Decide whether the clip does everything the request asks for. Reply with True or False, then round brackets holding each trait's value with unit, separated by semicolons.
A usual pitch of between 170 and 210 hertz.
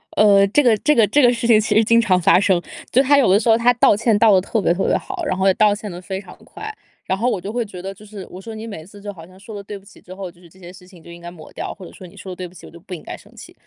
True (200 Hz)